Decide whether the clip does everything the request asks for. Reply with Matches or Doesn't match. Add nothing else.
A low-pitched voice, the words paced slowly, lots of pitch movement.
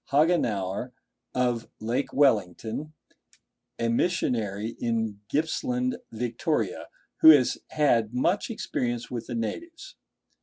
Matches